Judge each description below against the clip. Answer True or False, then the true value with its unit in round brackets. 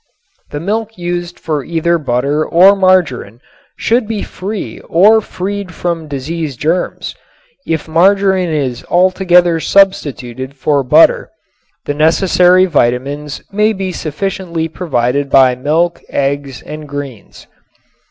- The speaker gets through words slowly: True (115 wpm)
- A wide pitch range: False (4.7 semitones)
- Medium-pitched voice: True (165 Hz)